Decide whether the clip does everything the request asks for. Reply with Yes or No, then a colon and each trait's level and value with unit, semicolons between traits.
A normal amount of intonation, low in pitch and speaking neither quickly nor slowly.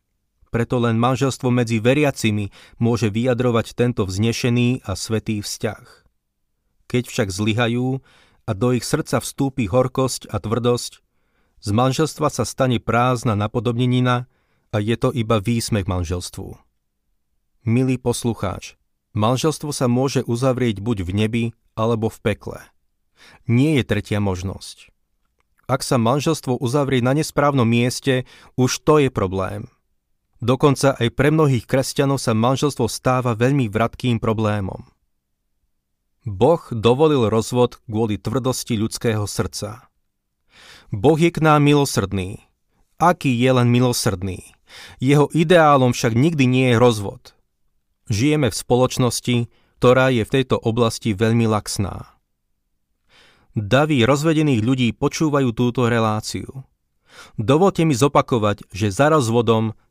Yes: average, 3.4 semitones; low, 120 Hz; average, 120 wpm